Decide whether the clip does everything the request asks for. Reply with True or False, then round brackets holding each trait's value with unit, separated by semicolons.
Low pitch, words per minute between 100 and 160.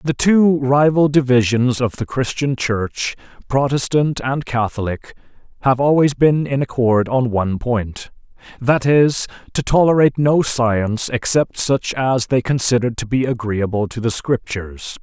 True (125 Hz; 145 wpm)